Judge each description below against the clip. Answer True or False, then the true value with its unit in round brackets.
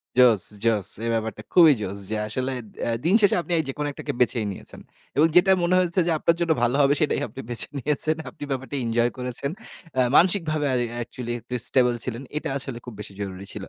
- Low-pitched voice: True (130 Hz)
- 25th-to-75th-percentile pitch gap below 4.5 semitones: False (5.0 semitones)